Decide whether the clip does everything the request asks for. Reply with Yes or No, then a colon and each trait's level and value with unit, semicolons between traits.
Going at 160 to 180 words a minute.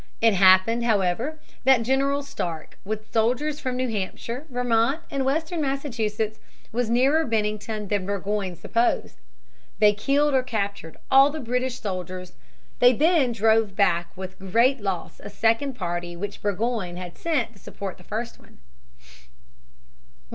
No: average, 140 wpm